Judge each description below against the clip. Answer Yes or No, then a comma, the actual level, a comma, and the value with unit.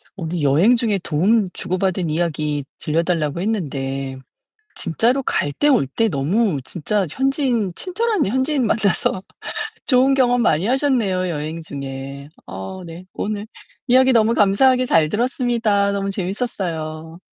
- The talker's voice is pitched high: Yes, high, 195 Hz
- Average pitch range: No, wide, 7.3 semitones